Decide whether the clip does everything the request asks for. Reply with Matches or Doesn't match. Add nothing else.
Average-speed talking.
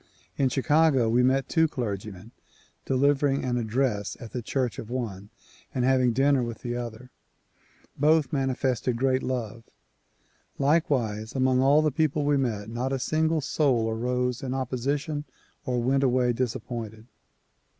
Matches